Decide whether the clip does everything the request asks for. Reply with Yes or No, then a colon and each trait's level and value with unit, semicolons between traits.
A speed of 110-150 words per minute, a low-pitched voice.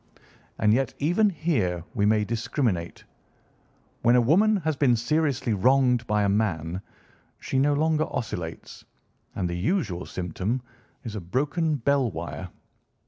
Yes: average, 140 wpm; low, 120 Hz